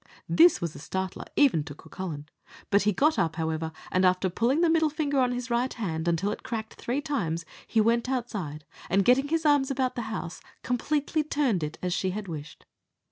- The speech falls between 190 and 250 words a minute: Yes, average, 200 wpm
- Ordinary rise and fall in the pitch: No, wide, 7.8 semitones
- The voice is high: Yes, high, 220 Hz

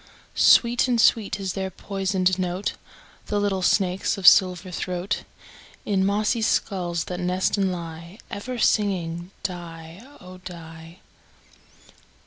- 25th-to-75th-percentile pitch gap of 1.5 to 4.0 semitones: Yes, narrow, 2.4 semitones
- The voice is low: No, medium, 185 Hz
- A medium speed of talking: No, slow, 120 wpm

